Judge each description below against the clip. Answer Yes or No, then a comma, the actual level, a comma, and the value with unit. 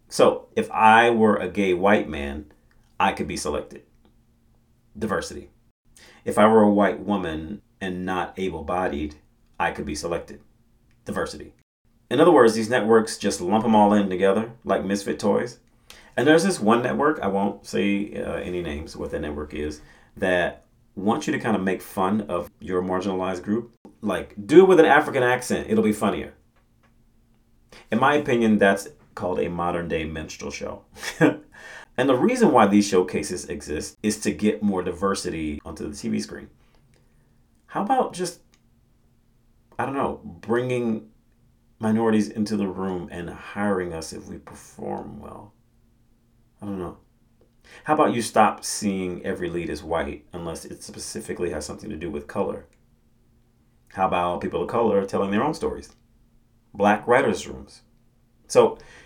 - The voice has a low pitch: Yes, low, 100 Hz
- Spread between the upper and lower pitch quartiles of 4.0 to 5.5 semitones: Yes, average, 4.5 semitones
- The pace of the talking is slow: No, average, 160 wpm